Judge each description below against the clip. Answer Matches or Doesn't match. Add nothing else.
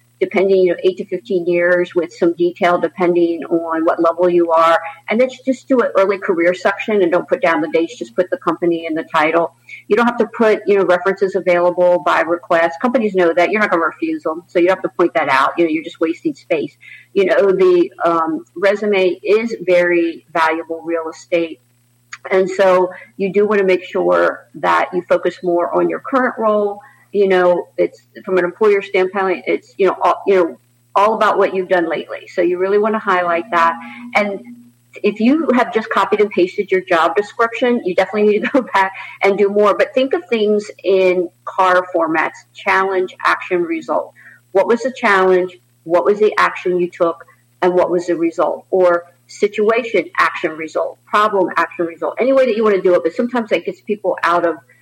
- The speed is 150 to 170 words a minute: Doesn't match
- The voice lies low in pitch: Doesn't match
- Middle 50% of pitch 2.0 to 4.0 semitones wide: Matches